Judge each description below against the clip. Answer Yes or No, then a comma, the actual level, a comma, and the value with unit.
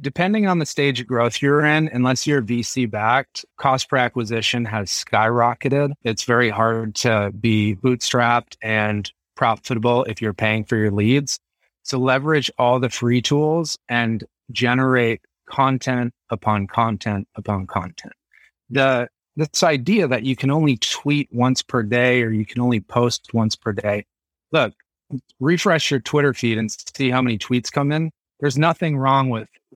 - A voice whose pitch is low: Yes, low, 125 Hz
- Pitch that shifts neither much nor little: Yes, average, 3.7 semitones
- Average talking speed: Yes, average, 160 wpm